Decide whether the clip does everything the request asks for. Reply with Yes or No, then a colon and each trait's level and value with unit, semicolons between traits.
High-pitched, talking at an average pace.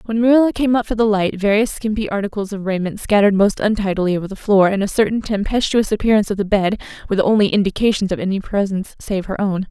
No: high, 205 Hz; fast, 225 wpm